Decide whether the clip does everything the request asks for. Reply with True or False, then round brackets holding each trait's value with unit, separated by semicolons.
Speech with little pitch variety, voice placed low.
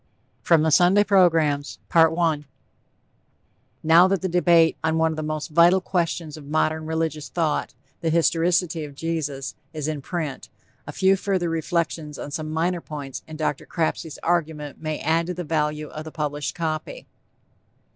False (2.0 semitones; 160 Hz)